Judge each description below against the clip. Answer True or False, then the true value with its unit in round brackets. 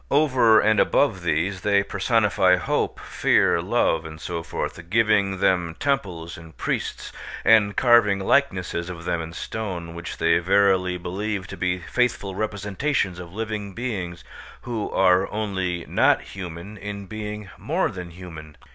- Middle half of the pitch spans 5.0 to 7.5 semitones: False (3.4 semitones)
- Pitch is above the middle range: False (95 Hz)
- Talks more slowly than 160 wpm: True (145 wpm)